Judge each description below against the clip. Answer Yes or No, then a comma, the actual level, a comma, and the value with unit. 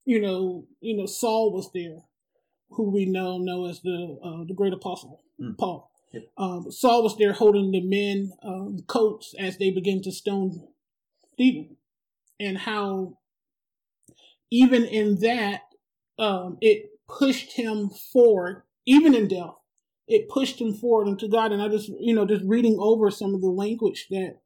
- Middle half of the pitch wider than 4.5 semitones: No, average, 3.3 semitones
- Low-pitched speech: No, high, 205 Hz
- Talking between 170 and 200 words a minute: No, average, 160 wpm